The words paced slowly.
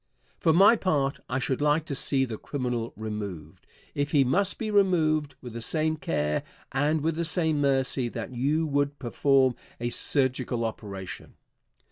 No: average, 160 wpm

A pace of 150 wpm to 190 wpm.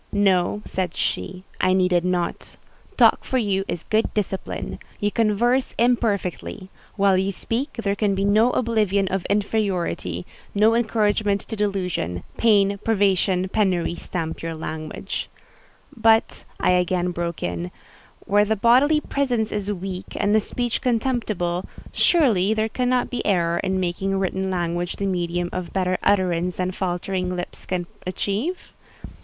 No: average, 140 wpm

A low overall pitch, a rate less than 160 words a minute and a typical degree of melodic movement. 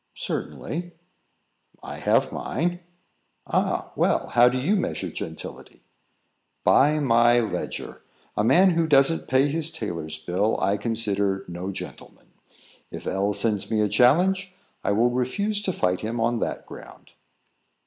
No: low, 120 Hz; average, 140 wpm; wide, 7.9 semitones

